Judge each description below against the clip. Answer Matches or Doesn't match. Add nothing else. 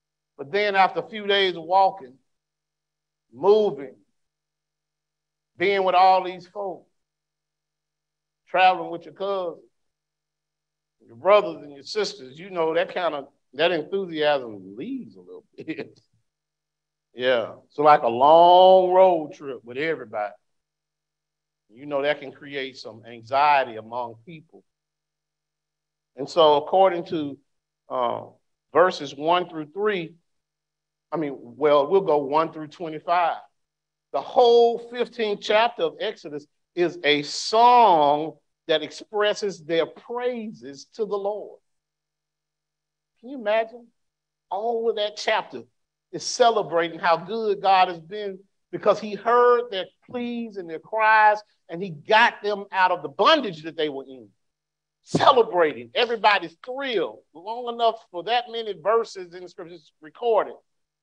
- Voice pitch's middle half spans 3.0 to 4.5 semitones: Doesn't match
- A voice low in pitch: Doesn't match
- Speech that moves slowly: Matches